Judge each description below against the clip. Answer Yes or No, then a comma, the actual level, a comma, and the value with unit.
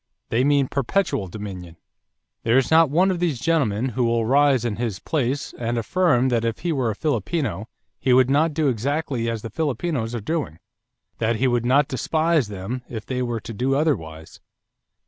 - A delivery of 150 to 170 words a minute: No, average, 185 wpm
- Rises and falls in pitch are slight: No, average, 4.4 semitones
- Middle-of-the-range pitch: No, low, 125 Hz